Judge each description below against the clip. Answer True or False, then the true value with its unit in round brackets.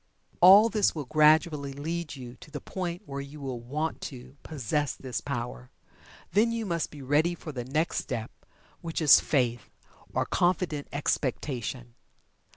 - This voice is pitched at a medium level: True (145 Hz)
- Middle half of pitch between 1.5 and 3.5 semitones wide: False (4.6 semitones)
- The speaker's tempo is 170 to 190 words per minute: False (155 wpm)